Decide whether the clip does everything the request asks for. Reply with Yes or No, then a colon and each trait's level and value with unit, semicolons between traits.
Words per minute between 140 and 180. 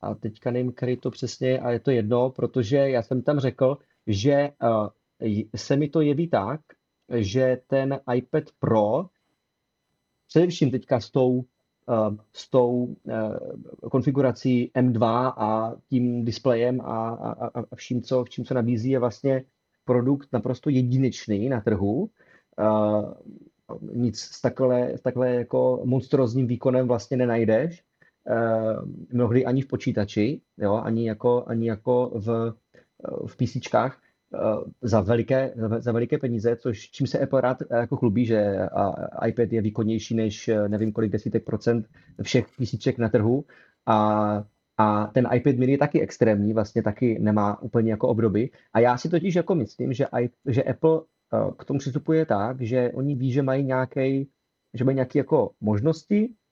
Yes: average, 150 wpm